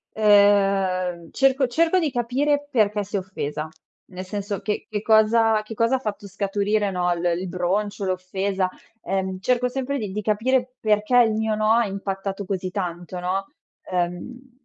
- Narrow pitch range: No, average, 3.4 semitones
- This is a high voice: Yes, high, 205 Hz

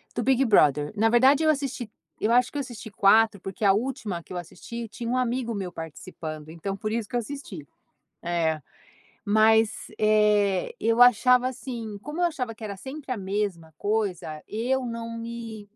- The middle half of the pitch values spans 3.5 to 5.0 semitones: Yes, average, 3.9 semitones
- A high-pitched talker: Yes, high, 220 Hz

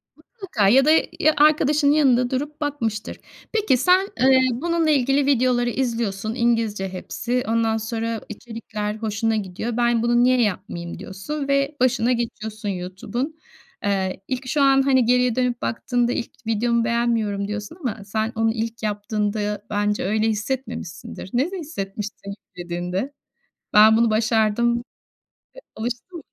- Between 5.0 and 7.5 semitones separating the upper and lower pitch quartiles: No, average, 3.6 semitones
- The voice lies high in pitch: Yes, high, 235 Hz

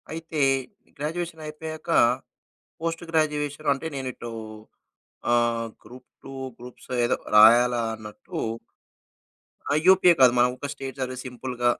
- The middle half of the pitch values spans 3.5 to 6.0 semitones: Yes, average, 4.4 semitones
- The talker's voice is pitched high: No, low, 135 Hz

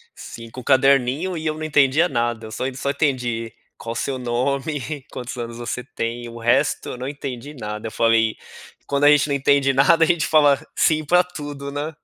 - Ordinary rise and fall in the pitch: Yes, average, 3.6 semitones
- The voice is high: No, low, 135 Hz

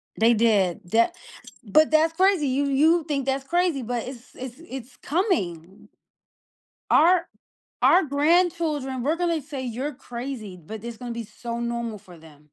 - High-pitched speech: Yes, very high, 260 Hz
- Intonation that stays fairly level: No, average, 5.3 semitones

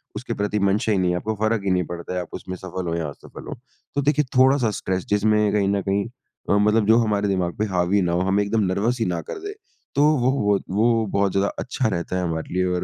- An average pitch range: Yes, average, 3.2 semitones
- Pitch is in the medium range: No, low, 100 Hz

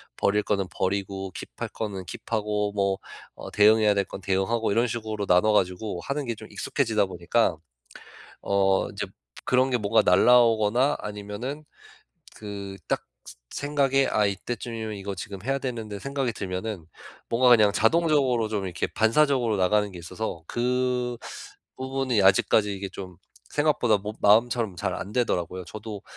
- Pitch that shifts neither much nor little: Yes, average, 3.7 semitones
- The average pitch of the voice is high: No, low, 105 Hz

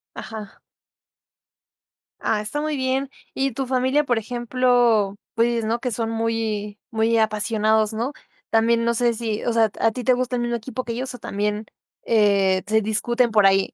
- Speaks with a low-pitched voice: No, high, 230 Hz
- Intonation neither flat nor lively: No, narrow, 2.3 semitones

